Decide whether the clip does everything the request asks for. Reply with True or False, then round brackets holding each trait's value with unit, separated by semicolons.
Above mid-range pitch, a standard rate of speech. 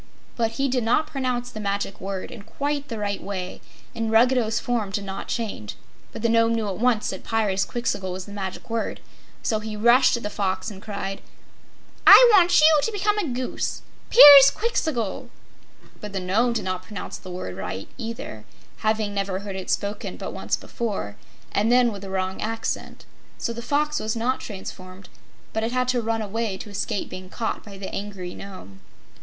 True (220 Hz; 185 wpm)